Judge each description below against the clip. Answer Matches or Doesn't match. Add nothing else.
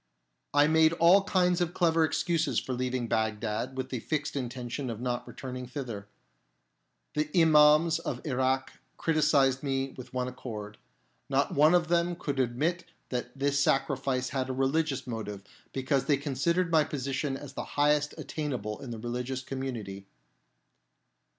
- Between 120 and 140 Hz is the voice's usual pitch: Matches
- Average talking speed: Matches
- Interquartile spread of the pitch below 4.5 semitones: Matches